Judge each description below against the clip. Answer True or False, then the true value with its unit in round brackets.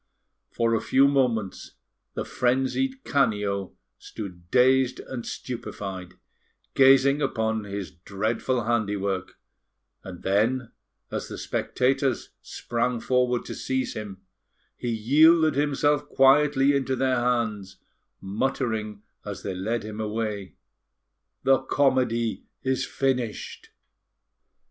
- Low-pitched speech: True (120 Hz)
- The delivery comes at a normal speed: False (105 wpm)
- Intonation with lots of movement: False (4.2 semitones)